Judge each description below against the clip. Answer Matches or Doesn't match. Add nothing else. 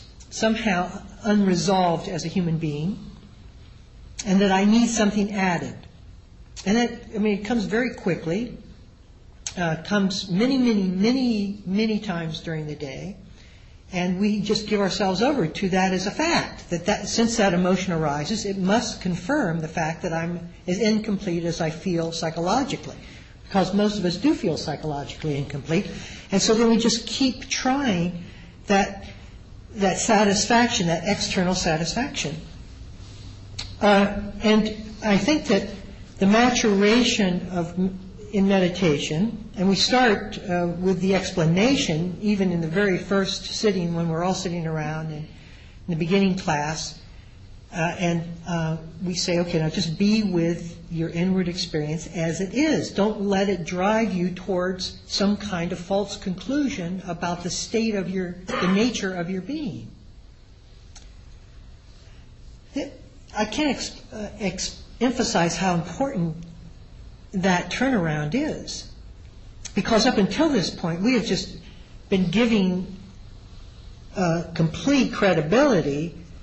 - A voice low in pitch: Doesn't match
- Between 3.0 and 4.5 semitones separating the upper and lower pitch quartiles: Matches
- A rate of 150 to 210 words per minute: Doesn't match